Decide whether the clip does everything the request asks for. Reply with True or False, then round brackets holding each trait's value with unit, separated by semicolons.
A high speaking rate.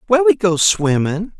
False (170 wpm)